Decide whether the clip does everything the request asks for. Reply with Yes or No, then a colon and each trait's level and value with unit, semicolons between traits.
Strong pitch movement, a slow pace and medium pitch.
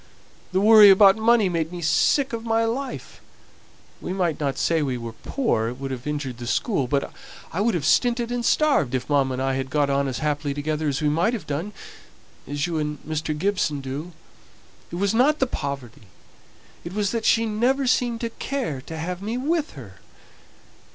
No: wide, 8.3 semitones; average, 200 wpm; medium, 165 Hz